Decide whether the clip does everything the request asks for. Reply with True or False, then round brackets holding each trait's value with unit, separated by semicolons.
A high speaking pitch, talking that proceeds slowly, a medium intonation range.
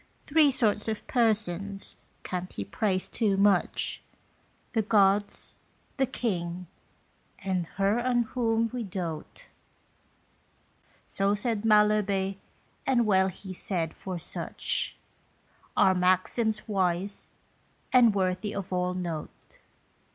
True (200 Hz; 105 wpm; 3.3 semitones)